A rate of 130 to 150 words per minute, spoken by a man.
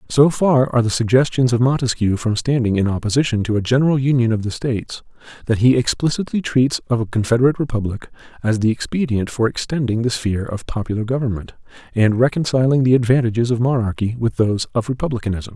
No: average, 175 wpm; male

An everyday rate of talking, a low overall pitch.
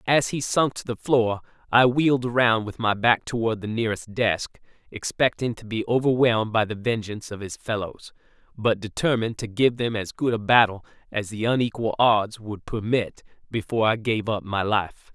Yes: average, 185 wpm; low, 115 Hz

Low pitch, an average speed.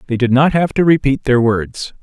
No: low, 130 Hz; fast, 235 wpm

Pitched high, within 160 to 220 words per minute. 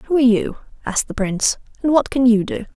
No: high, 240 Hz; fast, 235 wpm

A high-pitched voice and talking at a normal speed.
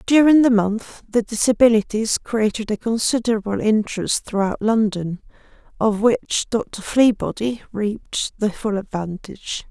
No: high, 220 Hz; slow, 120 wpm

